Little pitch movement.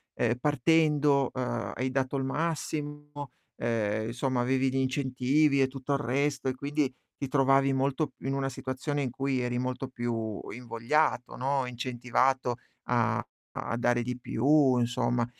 Yes: narrow, 2.2 semitones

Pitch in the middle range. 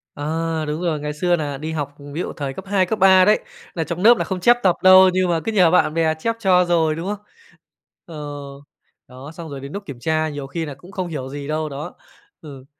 Yes: medium, 165 Hz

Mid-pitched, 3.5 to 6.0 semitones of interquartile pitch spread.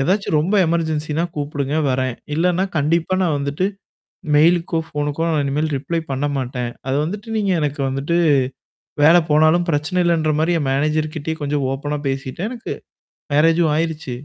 No: medium, 155 Hz; average, 2.8 semitones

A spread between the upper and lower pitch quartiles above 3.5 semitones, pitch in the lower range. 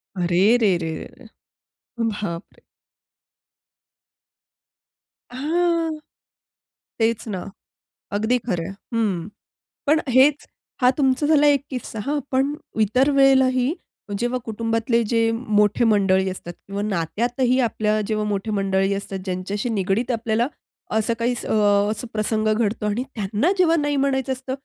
No: average, 4.2 semitones; high, 225 Hz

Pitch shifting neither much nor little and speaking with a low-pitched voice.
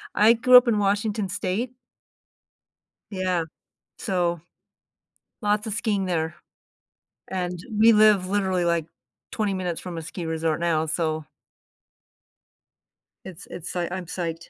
No: average, 3.5 semitones; medium, 185 Hz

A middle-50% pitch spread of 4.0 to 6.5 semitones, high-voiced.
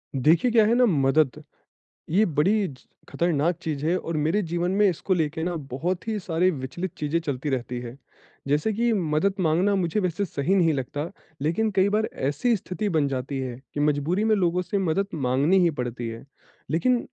No: average, 5.0 semitones; medium, 165 Hz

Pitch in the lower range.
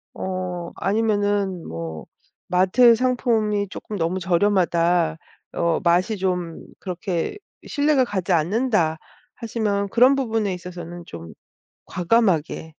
No: medium, 185 Hz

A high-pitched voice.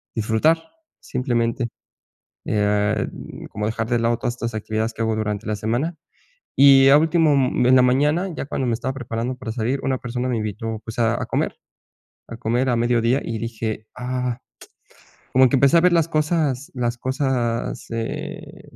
No: low, 120 Hz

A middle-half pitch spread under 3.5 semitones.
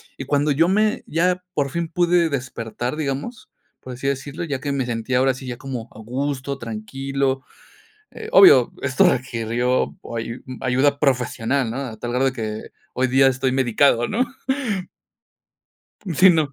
Yes: average, 2.9 semitones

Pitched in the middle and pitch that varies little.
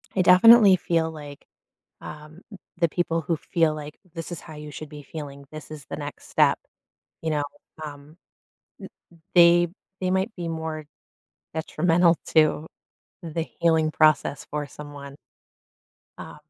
Yes: medium, 160 Hz; narrow, 2.3 semitones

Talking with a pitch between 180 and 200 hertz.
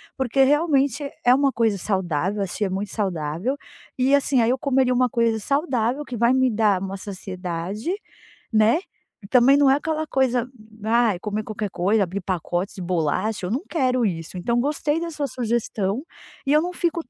No: high, 235 Hz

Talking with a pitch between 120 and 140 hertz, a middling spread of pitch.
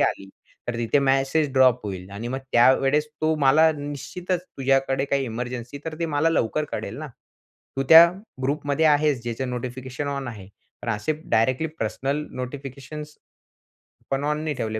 Yes: low, 135 Hz; average, 3.4 semitones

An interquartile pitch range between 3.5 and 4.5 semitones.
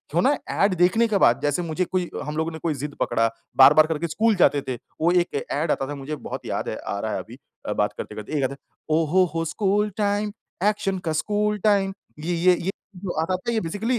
No: average, 5.2 semitones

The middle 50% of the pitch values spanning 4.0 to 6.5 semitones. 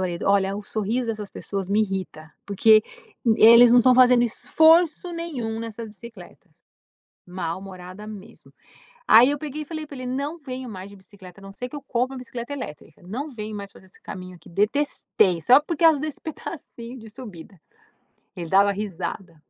Yes: average, 4.9 semitones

